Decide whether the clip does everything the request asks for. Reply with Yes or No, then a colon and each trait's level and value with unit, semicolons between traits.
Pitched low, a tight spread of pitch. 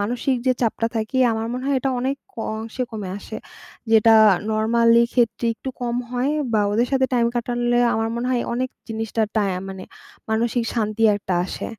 No: high, 230 Hz; narrow, 2.0 semitones